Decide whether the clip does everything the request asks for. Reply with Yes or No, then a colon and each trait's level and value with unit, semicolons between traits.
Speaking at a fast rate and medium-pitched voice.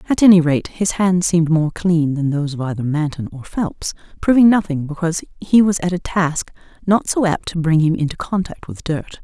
Yes: fast, 215 wpm; medium, 170 Hz